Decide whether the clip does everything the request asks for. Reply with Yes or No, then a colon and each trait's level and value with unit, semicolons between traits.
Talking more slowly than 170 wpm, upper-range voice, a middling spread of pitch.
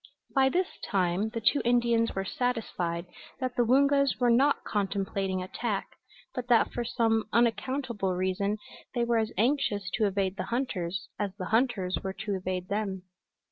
Yes: average, 160 wpm; high, 220 Hz; average, 4.1 semitones